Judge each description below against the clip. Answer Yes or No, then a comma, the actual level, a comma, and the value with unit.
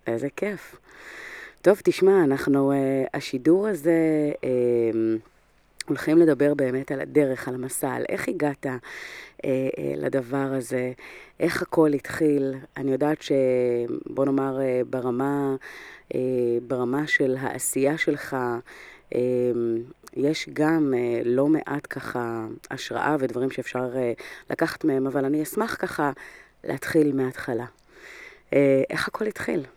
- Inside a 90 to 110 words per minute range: Yes, slow, 100 wpm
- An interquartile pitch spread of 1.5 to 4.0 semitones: Yes, narrow, 2.5 semitones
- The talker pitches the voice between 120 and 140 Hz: Yes, low, 135 Hz